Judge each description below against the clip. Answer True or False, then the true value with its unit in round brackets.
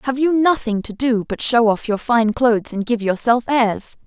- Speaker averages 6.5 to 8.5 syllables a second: False (4.7 syllables/s)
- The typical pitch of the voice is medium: False (235 Hz)